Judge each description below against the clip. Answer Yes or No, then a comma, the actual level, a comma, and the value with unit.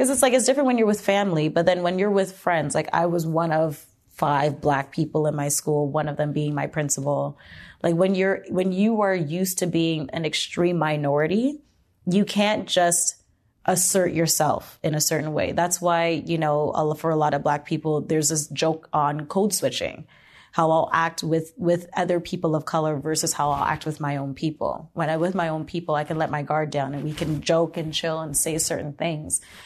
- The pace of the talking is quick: Yes, fast, 220 wpm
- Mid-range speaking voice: Yes, medium, 160 Hz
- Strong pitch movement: No, narrow, 2.6 semitones